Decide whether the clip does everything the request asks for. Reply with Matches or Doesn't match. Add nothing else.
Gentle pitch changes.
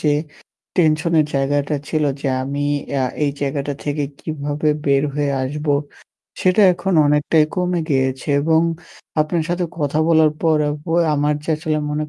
Matches